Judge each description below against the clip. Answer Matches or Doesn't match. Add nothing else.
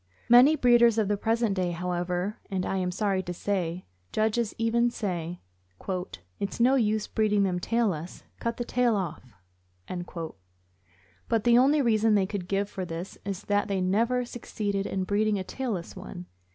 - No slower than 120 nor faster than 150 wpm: Doesn't match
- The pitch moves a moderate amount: Matches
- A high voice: Matches